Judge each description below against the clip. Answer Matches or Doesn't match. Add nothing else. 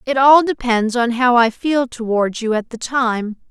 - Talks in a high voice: Matches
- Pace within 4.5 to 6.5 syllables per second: Doesn't match